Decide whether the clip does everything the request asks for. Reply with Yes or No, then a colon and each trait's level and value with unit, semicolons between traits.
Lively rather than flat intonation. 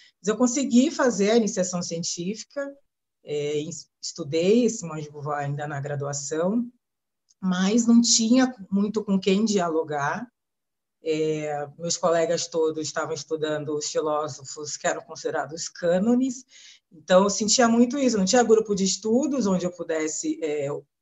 Yes: wide, 6.6 semitones